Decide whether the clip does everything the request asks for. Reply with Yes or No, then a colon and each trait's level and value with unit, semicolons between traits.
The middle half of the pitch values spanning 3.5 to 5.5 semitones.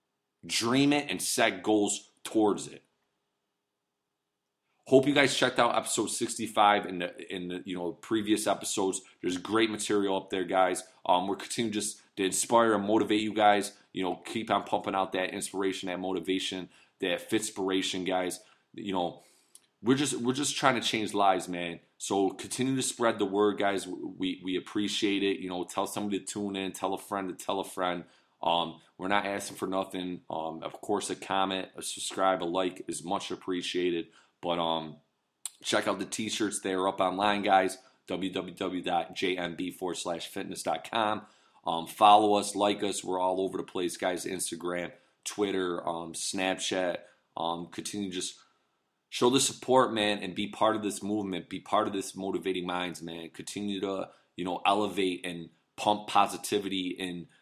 No: narrow, 2.5 semitones